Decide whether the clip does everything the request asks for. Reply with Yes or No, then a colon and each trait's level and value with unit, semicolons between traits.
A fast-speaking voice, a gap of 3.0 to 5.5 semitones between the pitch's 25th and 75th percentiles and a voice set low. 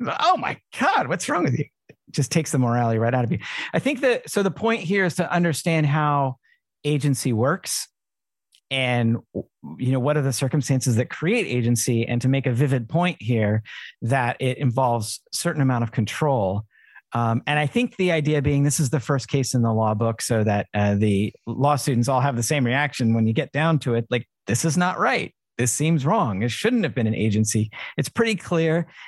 Yes: fast, 210 wpm; average, 4.8 semitones; low, 130 Hz